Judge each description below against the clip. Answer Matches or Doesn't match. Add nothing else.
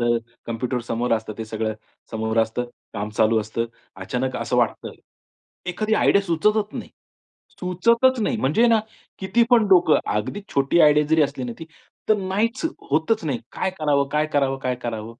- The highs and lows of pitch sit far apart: Matches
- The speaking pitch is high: Doesn't match